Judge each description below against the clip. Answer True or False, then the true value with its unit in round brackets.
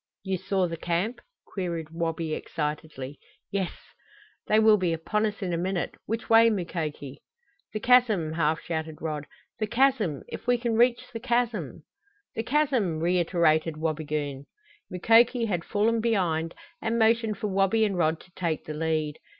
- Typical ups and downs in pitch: False (5.8 semitones)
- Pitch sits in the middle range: True (180 Hz)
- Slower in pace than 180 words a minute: True (160 wpm)